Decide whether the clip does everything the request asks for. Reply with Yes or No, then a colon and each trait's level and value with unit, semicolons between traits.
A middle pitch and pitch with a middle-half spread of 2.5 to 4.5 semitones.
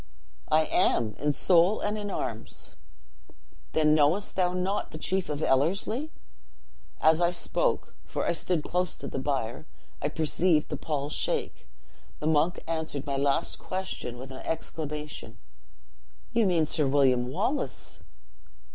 Yes: medium, 155 Hz; average, 4.2 semitones